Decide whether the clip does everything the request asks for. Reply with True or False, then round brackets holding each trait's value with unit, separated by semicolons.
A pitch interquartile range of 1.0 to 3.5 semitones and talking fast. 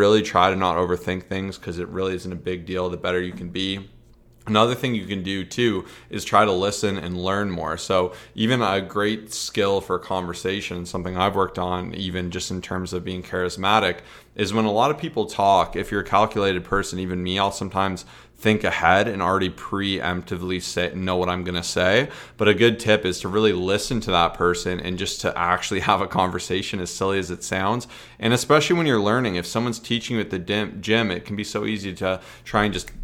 True (2.9 semitones; 220 wpm)